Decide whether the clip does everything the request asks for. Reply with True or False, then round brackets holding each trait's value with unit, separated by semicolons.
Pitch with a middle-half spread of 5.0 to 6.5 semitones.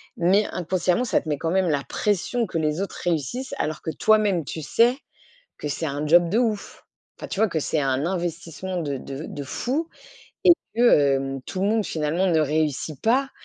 True (5.6 semitones)